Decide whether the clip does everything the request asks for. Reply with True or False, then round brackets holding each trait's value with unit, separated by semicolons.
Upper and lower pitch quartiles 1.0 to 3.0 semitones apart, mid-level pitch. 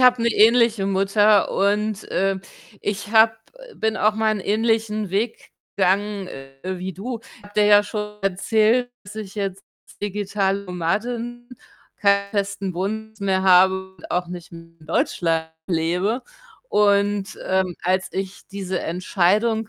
False (2.5 semitones; 200 Hz)